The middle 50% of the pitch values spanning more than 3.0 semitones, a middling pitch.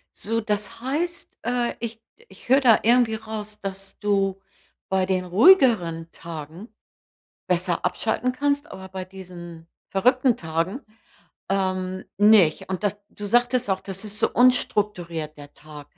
No: average, 4.2 semitones; high, 200 Hz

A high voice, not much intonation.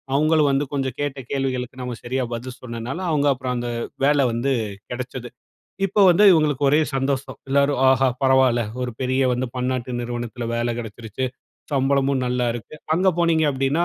No: low, 130 Hz; narrow, 2.3 semitones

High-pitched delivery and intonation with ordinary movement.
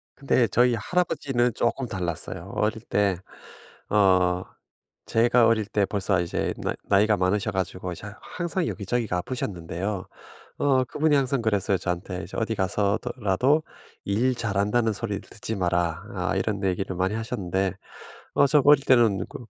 No: low, 105 Hz; average, 4.3 semitones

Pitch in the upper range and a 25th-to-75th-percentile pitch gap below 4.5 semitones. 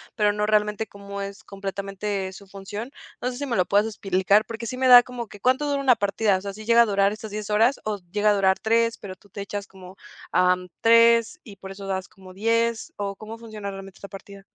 Yes: high, 205 Hz; narrow, 2.6 semitones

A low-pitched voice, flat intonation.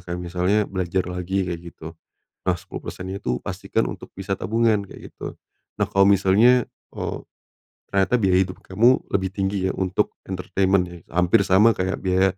Yes: very low, 95 Hz; narrow, 1.4 semitones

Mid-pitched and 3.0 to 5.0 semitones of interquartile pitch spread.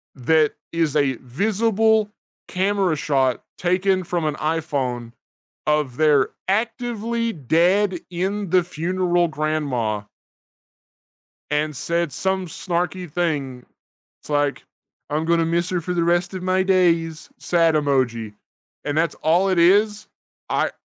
Yes: medium, 170 Hz; average, 3.9 semitones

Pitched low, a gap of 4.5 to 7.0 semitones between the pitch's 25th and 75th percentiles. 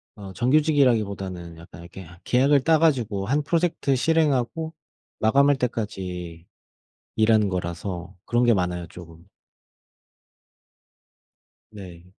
No: low, 105 Hz; wide, 7.5 semitones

